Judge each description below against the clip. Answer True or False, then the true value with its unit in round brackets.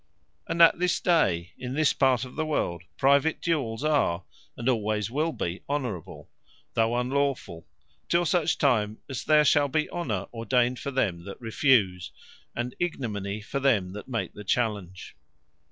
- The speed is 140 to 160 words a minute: True (155 wpm)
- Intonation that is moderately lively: False (5.8 semitones)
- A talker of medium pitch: False (125 Hz)